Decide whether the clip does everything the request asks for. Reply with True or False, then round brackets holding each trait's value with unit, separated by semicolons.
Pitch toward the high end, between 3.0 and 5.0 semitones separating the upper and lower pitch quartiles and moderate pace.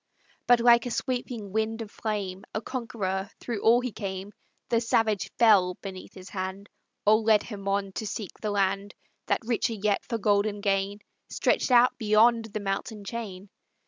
False (210 Hz; 2.5 semitones; 170 wpm)